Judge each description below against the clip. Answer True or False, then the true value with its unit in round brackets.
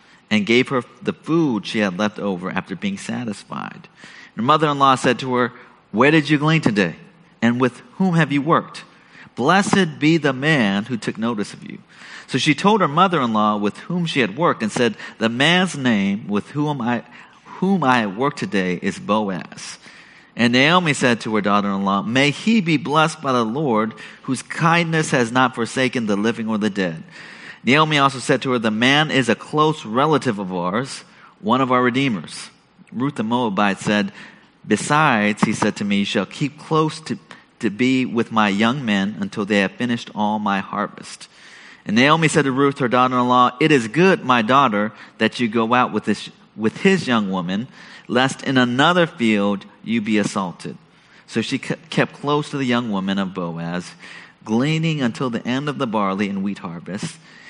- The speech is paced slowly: False (185 wpm)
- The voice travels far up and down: True (6.1 semitones)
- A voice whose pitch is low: True (130 Hz)